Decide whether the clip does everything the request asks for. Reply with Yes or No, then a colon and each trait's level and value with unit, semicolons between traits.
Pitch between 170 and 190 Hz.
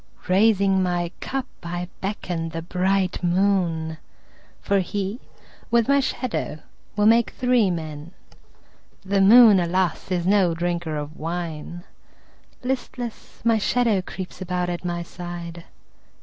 Yes: medium, 185 Hz